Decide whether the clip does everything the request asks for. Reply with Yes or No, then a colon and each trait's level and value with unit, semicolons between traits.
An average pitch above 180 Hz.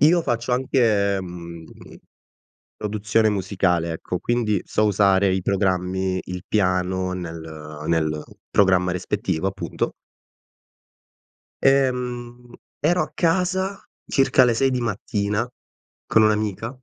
No: low, 100 Hz